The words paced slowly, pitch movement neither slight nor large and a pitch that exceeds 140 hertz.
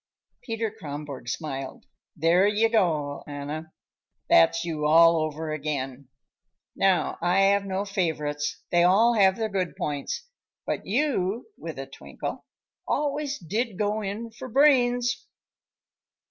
No: slow, 125 wpm; wide, 6.6 semitones; medium, 185 Hz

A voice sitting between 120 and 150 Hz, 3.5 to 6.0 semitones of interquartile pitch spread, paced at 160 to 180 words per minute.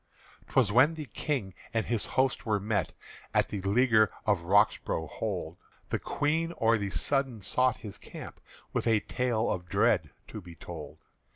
No: low, 110 Hz; average, 4.6 semitones; average, 170 wpm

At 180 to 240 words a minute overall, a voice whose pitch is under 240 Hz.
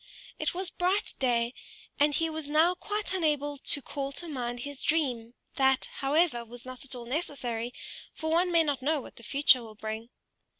No: average, 185 wpm; very high, 280 Hz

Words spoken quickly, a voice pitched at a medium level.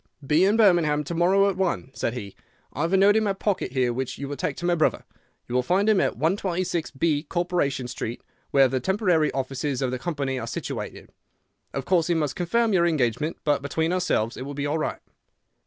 Yes: fast, 215 wpm; medium, 155 Hz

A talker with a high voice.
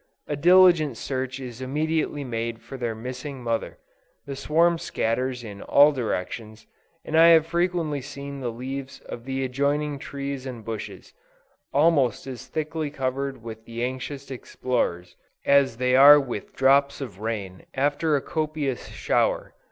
No: low, 135 Hz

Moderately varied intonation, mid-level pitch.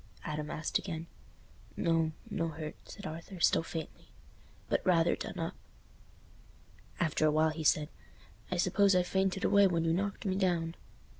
Yes: average, 3.0 semitones; medium, 165 Hz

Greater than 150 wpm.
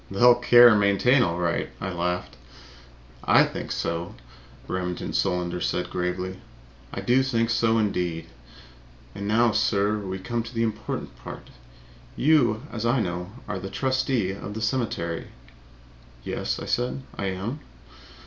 No: average, 145 wpm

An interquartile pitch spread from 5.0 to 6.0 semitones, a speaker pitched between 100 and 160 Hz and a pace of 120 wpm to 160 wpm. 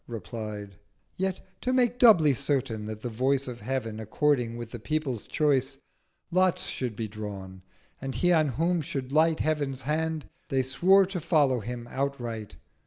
Yes: average, 5.3 semitones; low, 135 Hz; average, 155 wpm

